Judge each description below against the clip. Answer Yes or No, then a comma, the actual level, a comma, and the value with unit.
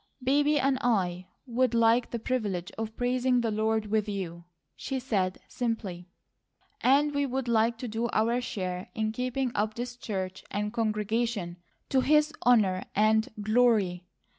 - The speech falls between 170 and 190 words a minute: No, average, 150 wpm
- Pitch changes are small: No, average, 3.3 semitones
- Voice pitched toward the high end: Yes, high, 225 Hz